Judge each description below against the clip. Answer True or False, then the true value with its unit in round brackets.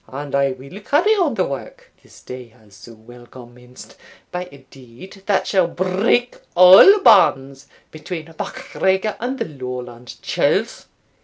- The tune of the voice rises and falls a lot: True (7.3 semitones)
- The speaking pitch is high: False (145 Hz)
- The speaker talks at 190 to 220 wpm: False (145 wpm)